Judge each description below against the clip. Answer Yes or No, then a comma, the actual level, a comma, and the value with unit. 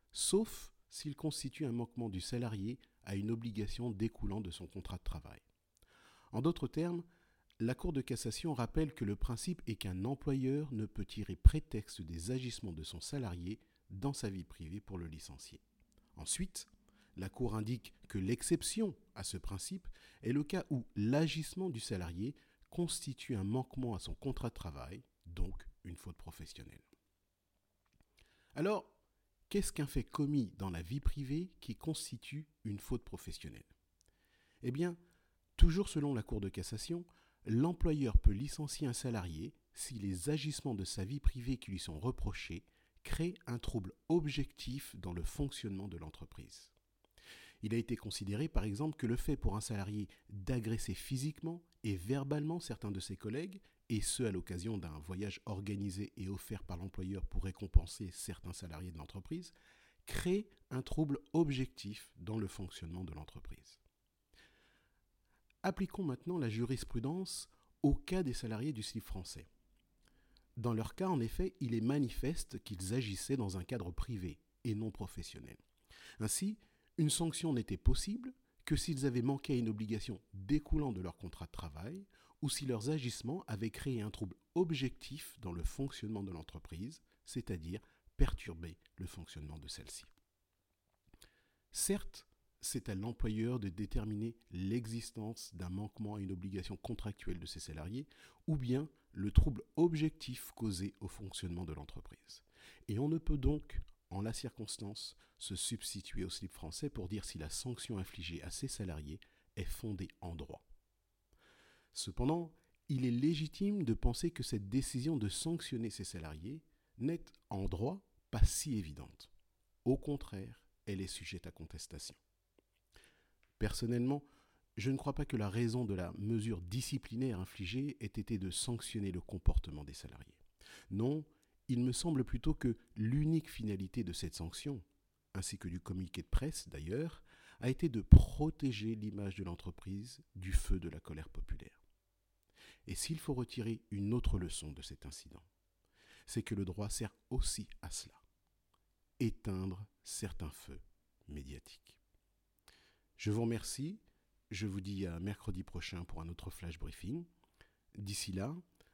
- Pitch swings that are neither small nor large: No, wide, 6.1 semitones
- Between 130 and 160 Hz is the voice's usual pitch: No, low, 110 Hz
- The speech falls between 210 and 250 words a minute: No, average, 150 wpm